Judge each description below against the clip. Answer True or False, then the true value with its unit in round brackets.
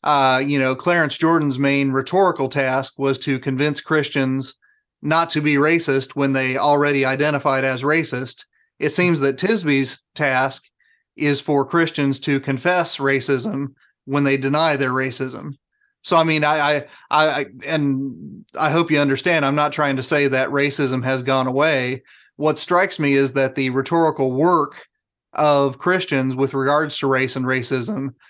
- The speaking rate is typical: True (160 wpm)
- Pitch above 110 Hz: True (140 Hz)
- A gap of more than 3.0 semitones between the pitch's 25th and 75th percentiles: False (2.4 semitones)